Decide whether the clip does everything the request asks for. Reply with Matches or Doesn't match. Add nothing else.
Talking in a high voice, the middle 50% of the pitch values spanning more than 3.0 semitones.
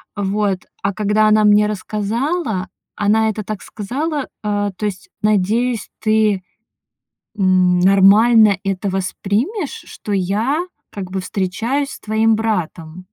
Doesn't match